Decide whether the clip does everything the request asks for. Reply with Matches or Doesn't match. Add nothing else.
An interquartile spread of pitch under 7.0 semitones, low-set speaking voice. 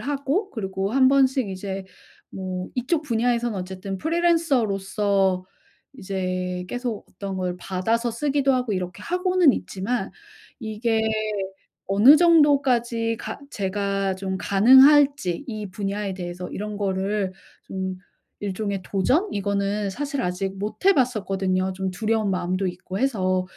Doesn't match